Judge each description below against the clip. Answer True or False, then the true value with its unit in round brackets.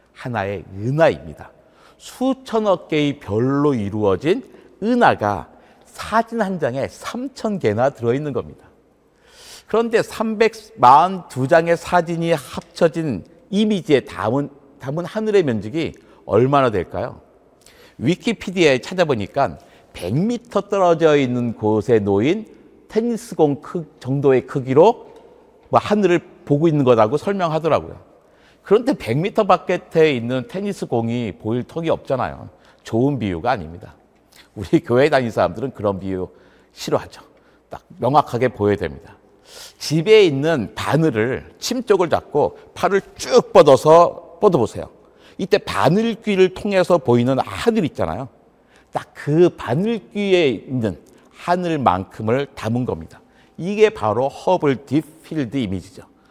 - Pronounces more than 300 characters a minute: False (270 characters per minute)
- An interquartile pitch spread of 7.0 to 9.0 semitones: True (8.5 semitones)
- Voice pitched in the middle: True (160 Hz)